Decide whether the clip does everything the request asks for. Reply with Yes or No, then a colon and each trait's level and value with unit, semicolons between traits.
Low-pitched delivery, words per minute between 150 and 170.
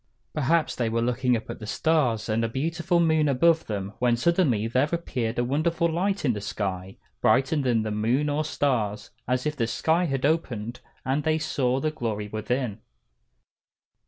No: low, 130 Hz; average, 180 wpm